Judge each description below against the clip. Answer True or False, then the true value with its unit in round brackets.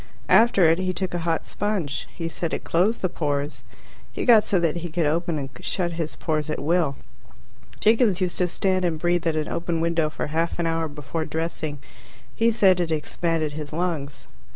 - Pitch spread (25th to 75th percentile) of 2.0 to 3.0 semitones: True (2.5 semitones)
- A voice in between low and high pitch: True (165 Hz)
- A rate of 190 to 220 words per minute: True (200 wpm)